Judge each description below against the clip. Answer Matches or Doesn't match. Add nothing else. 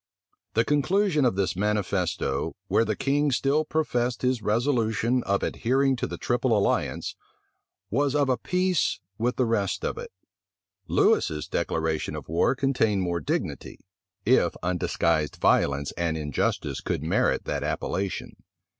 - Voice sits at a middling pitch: Doesn't match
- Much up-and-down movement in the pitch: Matches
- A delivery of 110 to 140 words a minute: Matches